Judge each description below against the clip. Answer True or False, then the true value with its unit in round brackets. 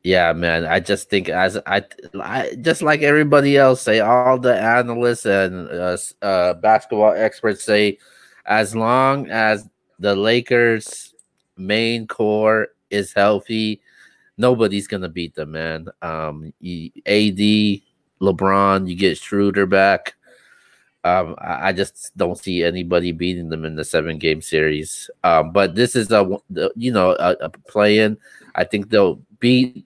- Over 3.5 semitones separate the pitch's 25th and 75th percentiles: True (4.1 semitones)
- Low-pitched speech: True (105 Hz)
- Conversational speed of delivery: True (150 wpm)